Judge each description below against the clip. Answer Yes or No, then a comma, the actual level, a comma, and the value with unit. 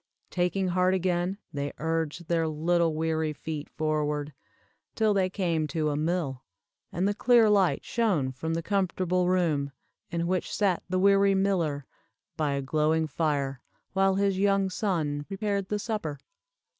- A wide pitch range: No, average, 3.9 semitones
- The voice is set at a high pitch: No, medium, 170 Hz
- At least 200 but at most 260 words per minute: No, average, 150 wpm